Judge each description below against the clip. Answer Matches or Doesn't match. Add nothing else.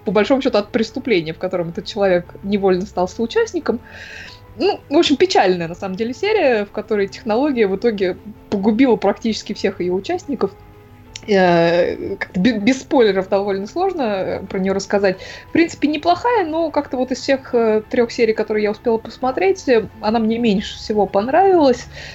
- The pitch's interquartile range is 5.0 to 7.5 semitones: Matches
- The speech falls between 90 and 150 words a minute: Doesn't match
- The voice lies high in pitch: Matches